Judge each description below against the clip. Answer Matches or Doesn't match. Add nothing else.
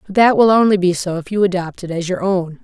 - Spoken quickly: Matches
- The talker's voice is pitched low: Doesn't match